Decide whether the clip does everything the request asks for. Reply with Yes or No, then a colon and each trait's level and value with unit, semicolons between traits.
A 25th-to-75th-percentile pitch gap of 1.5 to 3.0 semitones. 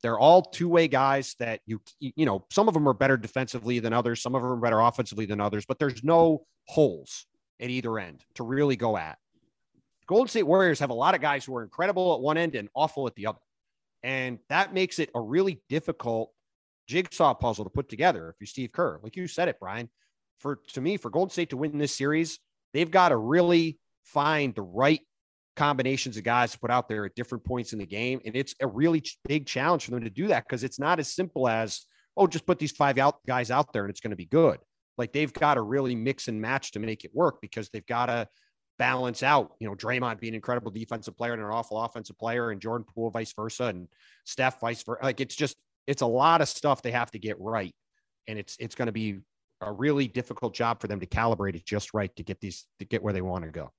No: average, 4.7 semitones